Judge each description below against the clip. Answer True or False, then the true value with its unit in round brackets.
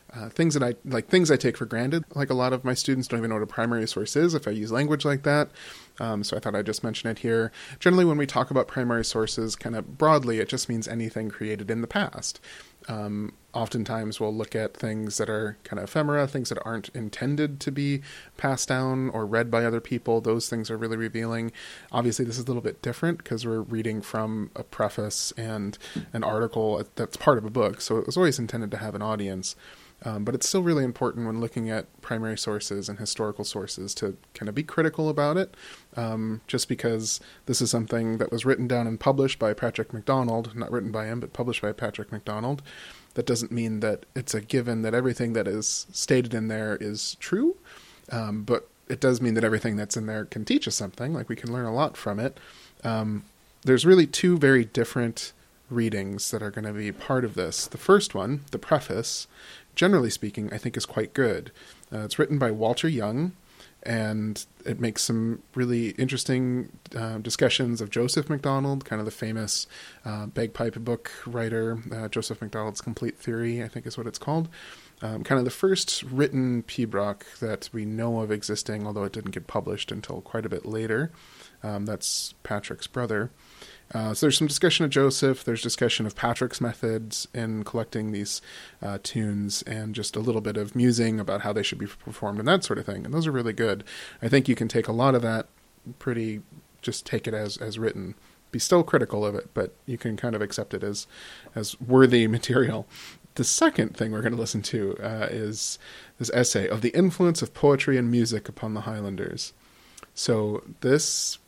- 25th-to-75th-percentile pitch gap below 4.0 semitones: True (3.0 semitones)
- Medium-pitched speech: False (115 Hz)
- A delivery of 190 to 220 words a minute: True (205 wpm)